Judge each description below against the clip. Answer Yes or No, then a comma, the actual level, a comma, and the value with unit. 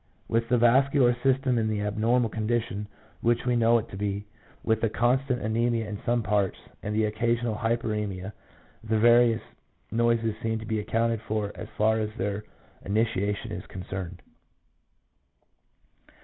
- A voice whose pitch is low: Yes, low, 110 Hz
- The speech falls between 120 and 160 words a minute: Yes, average, 150 wpm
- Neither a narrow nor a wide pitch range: No, narrow, 2.0 semitones